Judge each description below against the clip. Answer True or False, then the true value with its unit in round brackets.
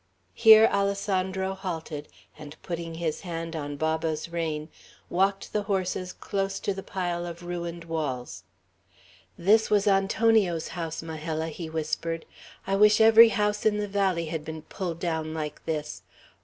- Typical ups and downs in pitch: True (3.5 semitones)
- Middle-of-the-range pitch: True (170 Hz)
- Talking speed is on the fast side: False (145 wpm)